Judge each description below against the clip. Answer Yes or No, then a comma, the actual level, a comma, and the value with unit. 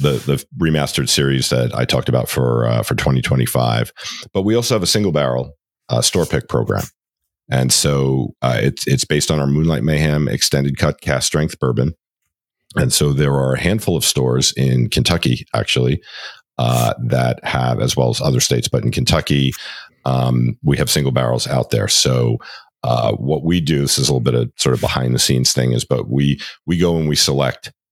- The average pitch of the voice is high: No, very low, 70 Hz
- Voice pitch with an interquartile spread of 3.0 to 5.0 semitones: Yes, average, 3.3 semitones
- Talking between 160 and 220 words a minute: Yes, average, 200 wpm